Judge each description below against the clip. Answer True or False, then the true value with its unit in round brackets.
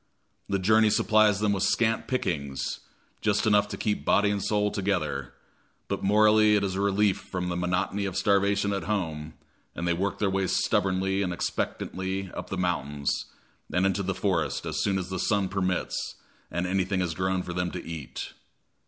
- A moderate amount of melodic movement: False (2.3 semitones)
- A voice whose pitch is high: False (95 Hz)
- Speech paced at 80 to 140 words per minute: False (180 wpm)